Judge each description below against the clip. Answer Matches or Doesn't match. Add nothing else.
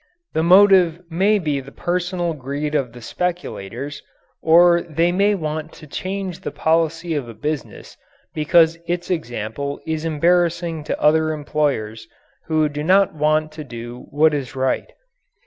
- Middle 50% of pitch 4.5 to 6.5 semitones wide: Doesn't match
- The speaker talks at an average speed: Matches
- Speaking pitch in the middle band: Matches